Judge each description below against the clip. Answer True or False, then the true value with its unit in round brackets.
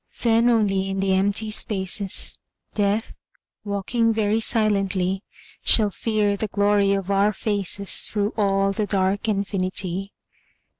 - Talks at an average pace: False (120 wpm)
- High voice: True (200 Hz)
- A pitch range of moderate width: False (1.6 semitones)